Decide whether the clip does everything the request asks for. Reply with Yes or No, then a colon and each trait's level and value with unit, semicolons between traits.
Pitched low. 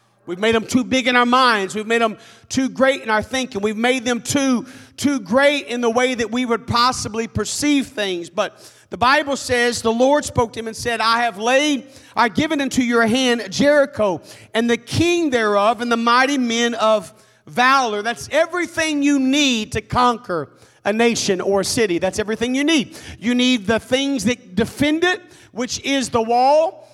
No: high, 240 Hz